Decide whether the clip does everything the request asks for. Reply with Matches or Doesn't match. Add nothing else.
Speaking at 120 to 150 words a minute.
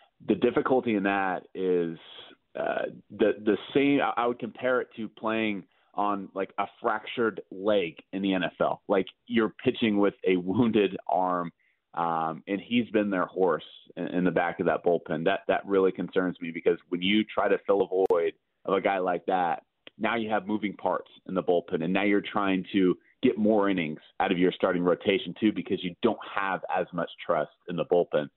Doesn't match